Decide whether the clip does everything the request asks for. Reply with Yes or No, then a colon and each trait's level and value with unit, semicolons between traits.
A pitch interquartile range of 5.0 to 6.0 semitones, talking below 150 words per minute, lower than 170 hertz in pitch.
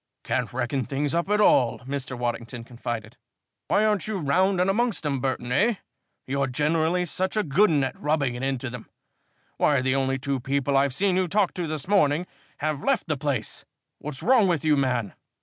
No: wide, 5.6 semitones; average, 195 wpm; medium, 140 Hz